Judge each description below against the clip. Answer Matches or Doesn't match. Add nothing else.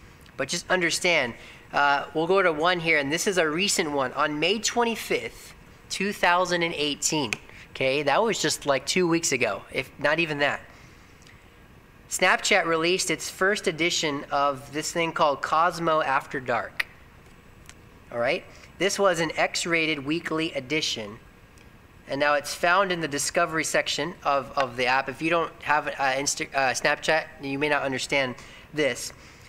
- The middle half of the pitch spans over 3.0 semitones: Matches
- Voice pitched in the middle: Matches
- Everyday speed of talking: Matches